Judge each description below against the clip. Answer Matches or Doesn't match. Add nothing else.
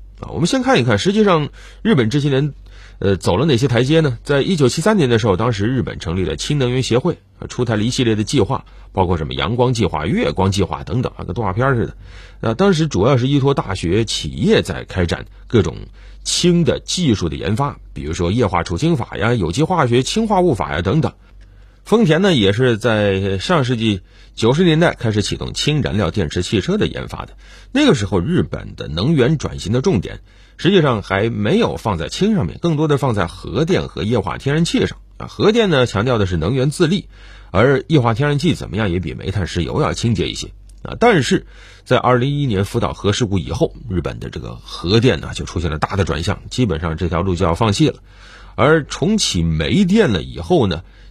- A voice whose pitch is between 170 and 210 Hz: Doesn't match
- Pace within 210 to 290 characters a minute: Doesn't match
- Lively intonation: Matches